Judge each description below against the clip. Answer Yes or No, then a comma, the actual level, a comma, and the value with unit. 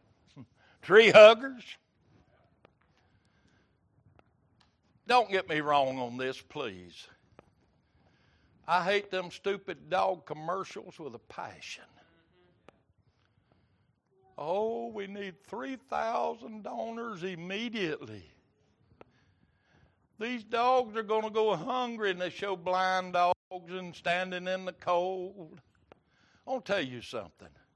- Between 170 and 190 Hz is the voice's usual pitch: Yes, medium, 185 Hz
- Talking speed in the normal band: No, slow, 95 wpm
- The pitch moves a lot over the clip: Yes, wide, 8.4 semitones